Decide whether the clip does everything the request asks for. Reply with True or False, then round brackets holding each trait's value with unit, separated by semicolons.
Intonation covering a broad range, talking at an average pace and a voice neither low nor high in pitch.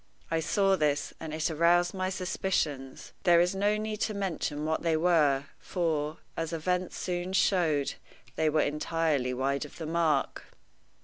False (3.1 semitones; 160 wpm; 165 Hz)